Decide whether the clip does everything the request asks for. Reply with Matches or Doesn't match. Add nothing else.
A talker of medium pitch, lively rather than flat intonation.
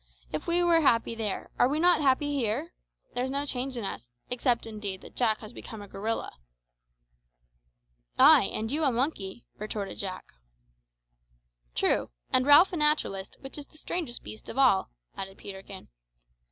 Doesn't match